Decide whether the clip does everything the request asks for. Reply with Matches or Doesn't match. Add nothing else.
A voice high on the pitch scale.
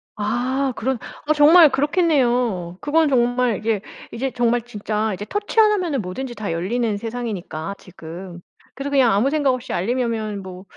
Matches